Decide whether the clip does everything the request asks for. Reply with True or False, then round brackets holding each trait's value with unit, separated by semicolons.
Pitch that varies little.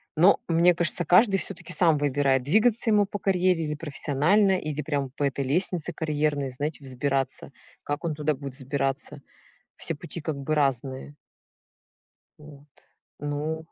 False (3.5 semitones)